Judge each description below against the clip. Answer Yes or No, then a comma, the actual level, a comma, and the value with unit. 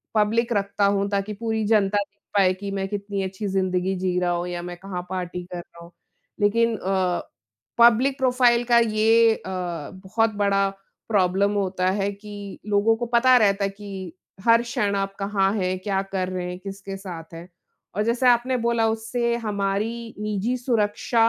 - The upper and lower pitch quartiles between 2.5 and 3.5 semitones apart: Yes, average, 2.9 semitones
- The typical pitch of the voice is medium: No, high, 200 Hz